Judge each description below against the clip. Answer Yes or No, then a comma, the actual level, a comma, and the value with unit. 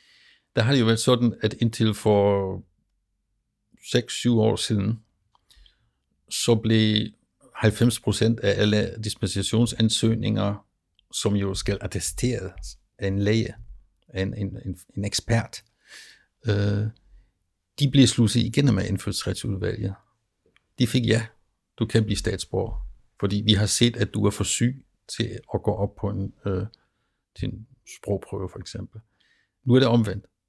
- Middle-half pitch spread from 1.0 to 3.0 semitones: Yes, narrow, 2.6 semitones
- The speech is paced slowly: Yes, slow, 135 wpm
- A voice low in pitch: Yes, low, 105 Hz